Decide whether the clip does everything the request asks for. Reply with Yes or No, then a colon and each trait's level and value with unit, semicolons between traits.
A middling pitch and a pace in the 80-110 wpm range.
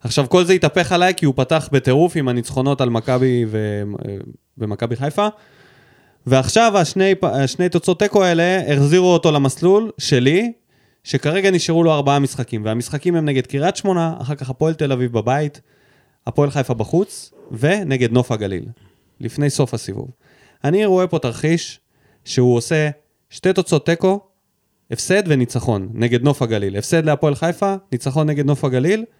No: medium, 145 Hz; average, 145 wpm